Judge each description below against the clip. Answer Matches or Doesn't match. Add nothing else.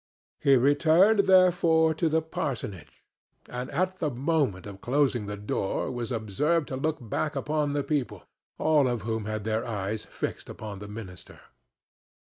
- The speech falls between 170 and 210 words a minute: Doesn't match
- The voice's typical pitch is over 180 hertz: Doesn't match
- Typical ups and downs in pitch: Doesn't match